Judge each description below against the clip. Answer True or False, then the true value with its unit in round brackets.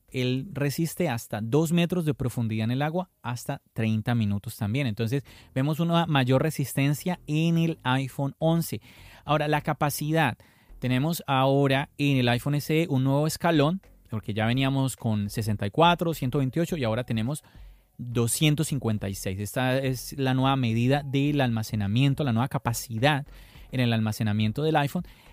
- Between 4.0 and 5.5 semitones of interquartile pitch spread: True (4.5 semitones)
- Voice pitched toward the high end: False (135 Hz)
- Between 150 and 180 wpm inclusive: False (140 wpm)